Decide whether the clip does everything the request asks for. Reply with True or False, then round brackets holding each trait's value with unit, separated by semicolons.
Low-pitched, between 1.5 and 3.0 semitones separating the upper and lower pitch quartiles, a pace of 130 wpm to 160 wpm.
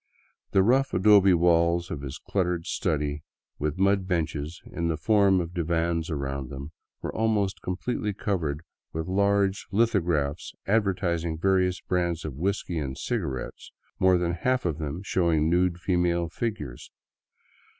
False (85 Hz; 3.4 semitones; 140 wpm)